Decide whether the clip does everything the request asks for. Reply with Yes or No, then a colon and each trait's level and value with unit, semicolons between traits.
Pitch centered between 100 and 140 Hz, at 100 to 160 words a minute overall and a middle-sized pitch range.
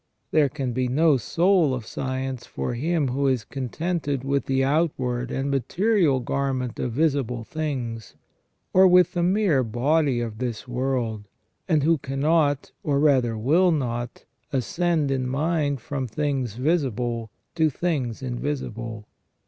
Yes: low, 135 Hz; average, 140 wpm; average, 4.1 semitones